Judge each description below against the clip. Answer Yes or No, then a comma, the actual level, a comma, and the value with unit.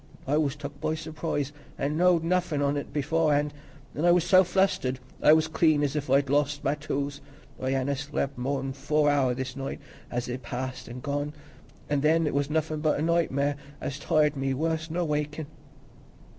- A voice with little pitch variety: Yes, narrow, 2.3 semitones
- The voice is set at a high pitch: No, medium, 145 Hz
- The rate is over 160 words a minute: Yes, average, 190 wpm